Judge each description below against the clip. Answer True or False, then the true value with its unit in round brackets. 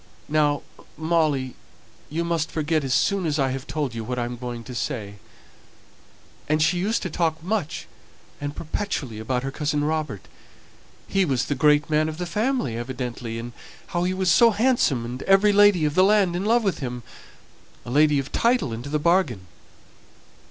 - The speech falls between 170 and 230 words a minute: True (180 wpm)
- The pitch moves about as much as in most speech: False (5.7 semitones)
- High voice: False (150 Hz)